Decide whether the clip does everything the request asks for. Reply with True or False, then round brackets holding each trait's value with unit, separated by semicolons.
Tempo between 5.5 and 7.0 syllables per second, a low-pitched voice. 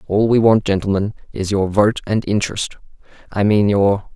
False (5.1 syllables/s; 100 Hz)